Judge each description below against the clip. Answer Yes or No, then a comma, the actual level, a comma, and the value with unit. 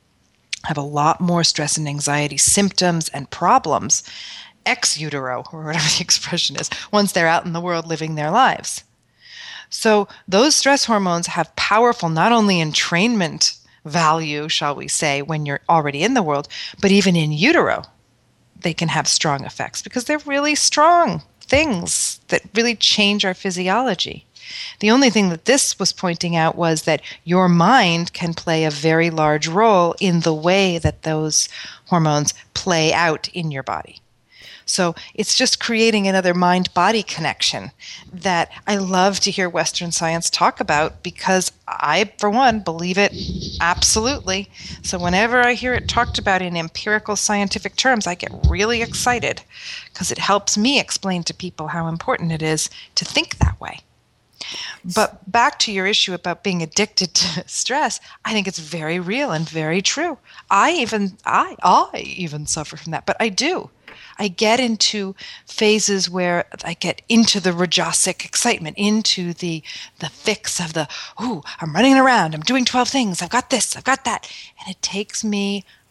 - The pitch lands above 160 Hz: Yes, medium, 185 Hz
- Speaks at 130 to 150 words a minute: No, average, 165 wpm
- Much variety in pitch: No, average, 4.7 semitones